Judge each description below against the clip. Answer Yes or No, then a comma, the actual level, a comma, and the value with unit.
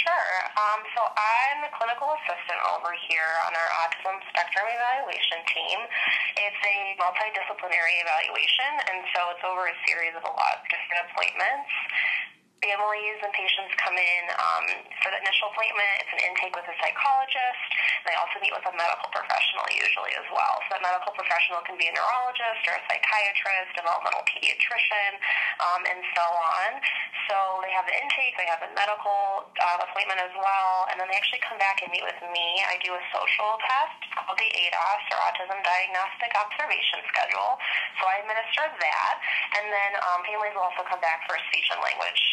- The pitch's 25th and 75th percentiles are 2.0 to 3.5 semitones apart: Yes, average, 3.1 semitones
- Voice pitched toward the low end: No, high, 195 Hz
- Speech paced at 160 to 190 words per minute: Yes, average, 185 wpm